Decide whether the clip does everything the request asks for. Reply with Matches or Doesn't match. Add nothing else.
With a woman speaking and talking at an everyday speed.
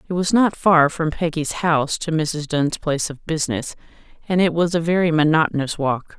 Matches